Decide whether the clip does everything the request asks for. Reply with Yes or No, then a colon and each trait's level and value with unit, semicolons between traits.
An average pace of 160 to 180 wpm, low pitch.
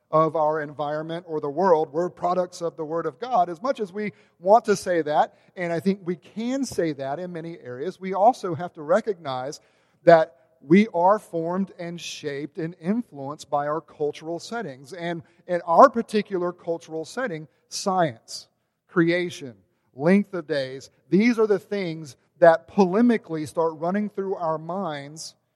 No: average, 165 wpm; medium, 170 Hz